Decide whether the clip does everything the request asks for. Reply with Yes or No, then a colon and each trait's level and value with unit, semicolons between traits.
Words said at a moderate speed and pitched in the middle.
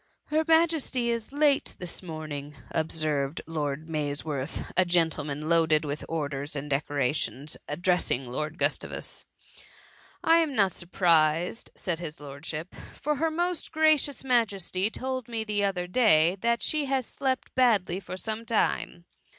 Yes: average, 150 wpm; medium, 175 Hz